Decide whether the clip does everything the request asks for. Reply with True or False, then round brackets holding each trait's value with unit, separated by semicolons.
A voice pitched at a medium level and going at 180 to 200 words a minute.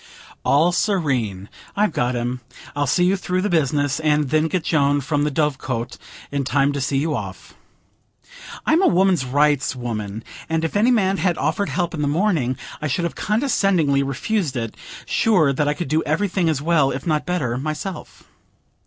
True (150 Hz; 185 wpm)